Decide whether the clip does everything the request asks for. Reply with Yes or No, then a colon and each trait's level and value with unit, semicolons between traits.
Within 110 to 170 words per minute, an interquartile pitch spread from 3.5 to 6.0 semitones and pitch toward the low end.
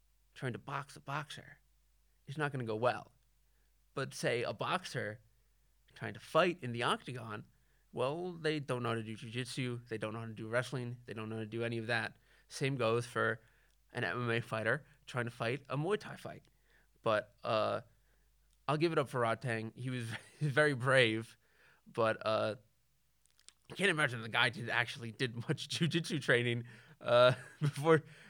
No: average, 180 wpm; average, 4.2 semitones; low, 125 Hz